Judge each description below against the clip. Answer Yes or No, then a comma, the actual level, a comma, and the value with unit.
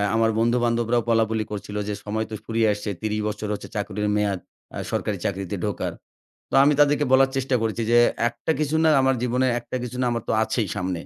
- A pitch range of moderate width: Yes, average, 3.0 semitones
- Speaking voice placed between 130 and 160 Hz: No, low, 115 Hz